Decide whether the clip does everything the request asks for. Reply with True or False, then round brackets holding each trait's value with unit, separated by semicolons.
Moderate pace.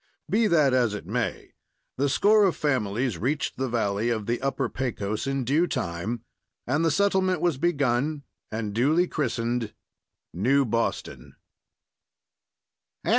False (130 wpm)